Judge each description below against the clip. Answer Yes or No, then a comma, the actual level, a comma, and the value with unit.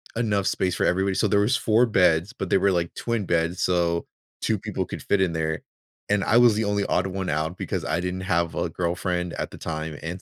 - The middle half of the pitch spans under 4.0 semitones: Yes, average, 3.2 semitones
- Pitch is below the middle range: Yes, very low, 90 Hz